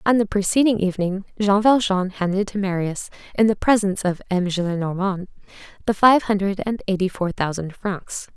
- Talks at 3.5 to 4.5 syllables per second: No, 5.4 syllables/s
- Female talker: Yes, female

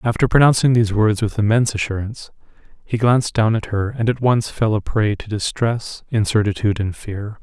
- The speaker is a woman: No, male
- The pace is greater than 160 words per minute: Yes, average, 185 wpm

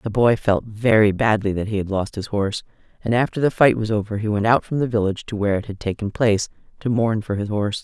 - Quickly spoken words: Yes, fast, 260 wpm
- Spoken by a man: No, female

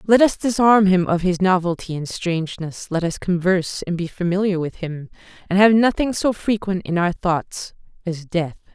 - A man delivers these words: No, female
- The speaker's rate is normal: Yes, average, 185 wpm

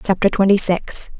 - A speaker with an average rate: Yes, average, 150 wpm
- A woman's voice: Yes, female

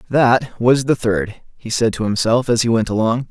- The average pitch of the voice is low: Yes, low, 115 Hz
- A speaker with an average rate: No, fast, 220 wpm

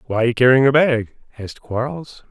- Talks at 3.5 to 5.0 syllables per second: Yes, 4.7 syllables/s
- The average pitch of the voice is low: Yes, low, 125 Hz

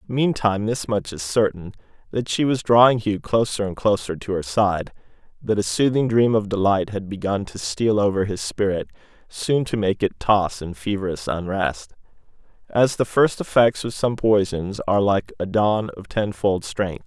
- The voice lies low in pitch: Yes, low, 100 Hz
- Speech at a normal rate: Yes, average, 180 wpm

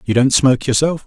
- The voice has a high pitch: No, low, 135 Hz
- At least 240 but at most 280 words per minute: No, fast, 225 wpm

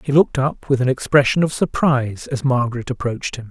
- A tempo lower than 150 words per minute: No, fast, 205 wpm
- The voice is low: Yes, low, 130 Hz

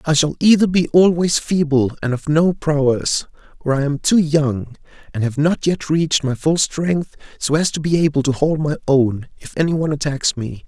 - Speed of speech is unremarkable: No, fast, 210 wpm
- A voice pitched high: No, medium, 150 Hz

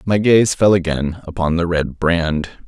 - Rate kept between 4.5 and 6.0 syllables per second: No, 4.1 syllables/s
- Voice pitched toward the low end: Yes, very low, 85 Hz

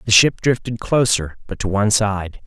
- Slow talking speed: No, average, 195 wpm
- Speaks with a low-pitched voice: Yes, low, 110 Hz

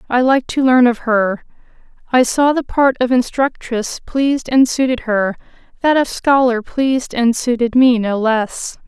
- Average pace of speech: Yes, average, 170 wpm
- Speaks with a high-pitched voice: Yes, high, 245 Hz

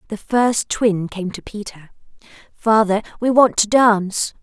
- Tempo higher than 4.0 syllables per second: Yes, 4.2 syllables/s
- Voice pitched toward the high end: Yes, high, 210 Hz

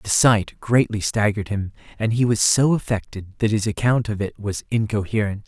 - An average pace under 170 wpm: No, average, 185 wpm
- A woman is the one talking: No, male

